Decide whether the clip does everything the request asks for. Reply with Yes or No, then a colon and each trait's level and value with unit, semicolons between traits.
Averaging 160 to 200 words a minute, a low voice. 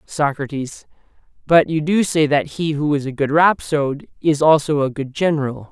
No: average, 180 wpm; medium, 150 Hz